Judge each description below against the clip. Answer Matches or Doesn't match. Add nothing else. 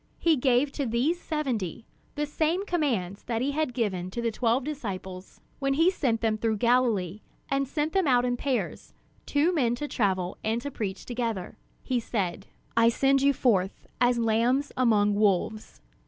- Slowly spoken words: Doesn't match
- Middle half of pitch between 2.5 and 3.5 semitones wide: Doesn't match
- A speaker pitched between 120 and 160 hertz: Doesn't match